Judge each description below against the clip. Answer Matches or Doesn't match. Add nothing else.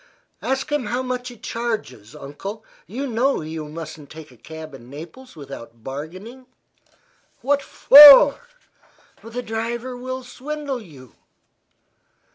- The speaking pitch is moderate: Doesn't match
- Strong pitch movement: Matches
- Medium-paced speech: Doesn't match